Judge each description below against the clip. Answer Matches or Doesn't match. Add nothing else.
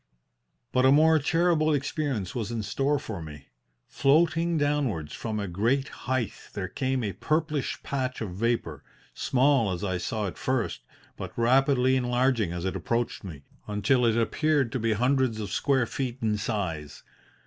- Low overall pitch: Matches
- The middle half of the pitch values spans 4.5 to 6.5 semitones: Matches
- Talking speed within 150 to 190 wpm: Matches